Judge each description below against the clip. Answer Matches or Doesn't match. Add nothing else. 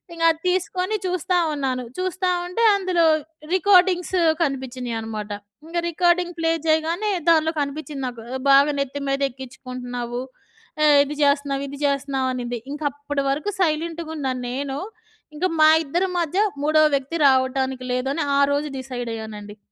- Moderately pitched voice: Doesn't match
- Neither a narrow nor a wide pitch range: Matches